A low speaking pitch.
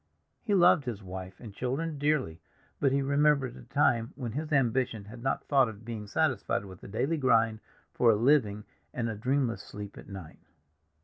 Yes: low, 120 Hz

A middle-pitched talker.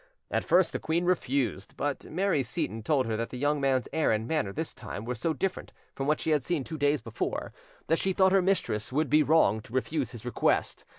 Yes: medium, 145 Hz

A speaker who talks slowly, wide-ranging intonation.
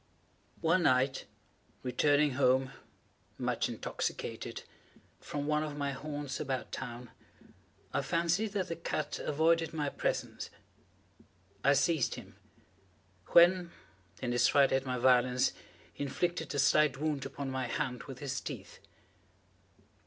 No: slow, 125 wpm; average, 3.1 semitones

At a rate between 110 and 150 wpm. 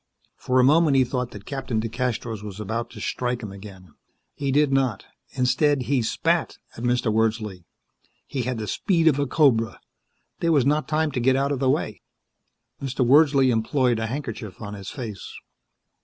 No: average, 180 wpm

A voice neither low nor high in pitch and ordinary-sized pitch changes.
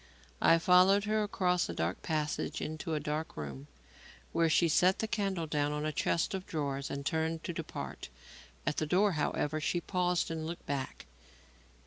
Yes: medium, 160 Hz; average, 3.3 semitones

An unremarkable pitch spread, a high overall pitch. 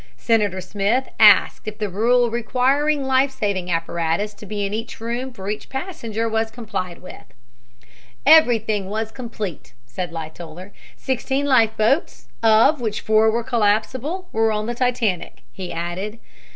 Yes: average, 3.8 semitones; high, 220 Hz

